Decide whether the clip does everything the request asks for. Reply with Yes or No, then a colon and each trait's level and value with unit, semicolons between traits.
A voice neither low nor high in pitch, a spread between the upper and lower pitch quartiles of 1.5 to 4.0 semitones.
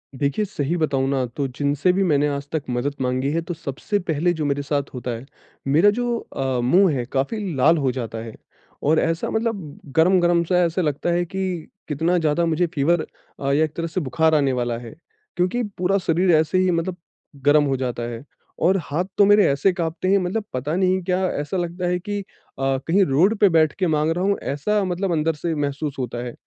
No: medium, 160 Hz; average, 4.5 semitones